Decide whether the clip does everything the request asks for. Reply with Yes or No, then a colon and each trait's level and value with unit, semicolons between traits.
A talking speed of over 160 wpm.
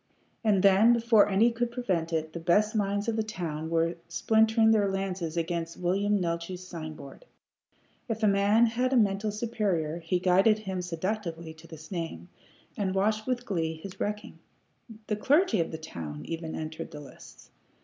Yes: average, 170 wpm